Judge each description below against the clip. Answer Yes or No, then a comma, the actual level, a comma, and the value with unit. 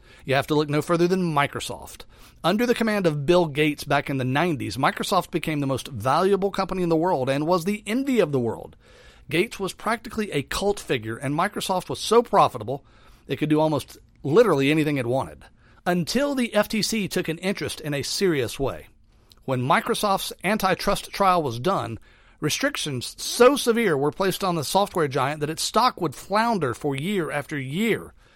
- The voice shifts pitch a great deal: Yes, wide, 6.4 semitones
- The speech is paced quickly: No, average, 185 wpm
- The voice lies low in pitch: No, medium, 165 Hz